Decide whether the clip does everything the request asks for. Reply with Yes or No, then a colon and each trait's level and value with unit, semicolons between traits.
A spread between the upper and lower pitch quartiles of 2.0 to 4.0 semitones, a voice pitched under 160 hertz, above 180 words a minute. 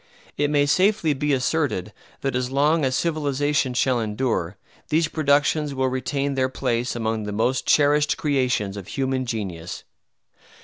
No: average, 3.5 semitones; low, 135 Hz; average, 145 wpm